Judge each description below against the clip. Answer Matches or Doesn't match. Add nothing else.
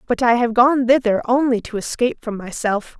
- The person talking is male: Doesn't match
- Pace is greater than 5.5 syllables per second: Doesn't match